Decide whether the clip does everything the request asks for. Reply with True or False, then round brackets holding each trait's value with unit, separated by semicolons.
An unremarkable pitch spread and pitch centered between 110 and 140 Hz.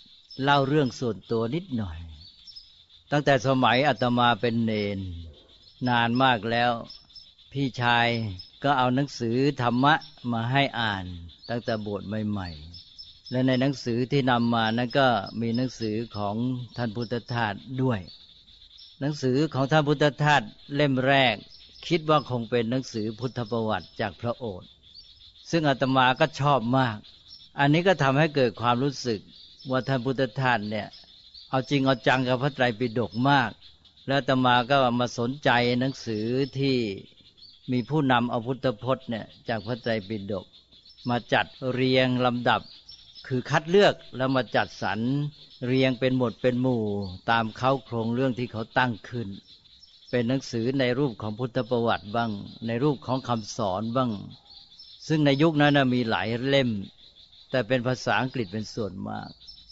True (3.5 semitones; 120 Hz)